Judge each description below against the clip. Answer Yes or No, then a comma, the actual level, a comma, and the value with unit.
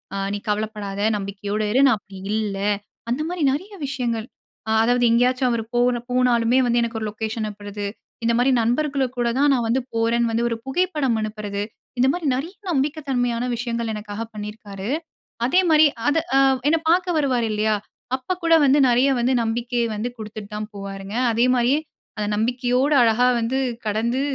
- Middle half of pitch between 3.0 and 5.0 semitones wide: Yes, average, 3.5 semitones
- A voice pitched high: Yes, high, 235 Hz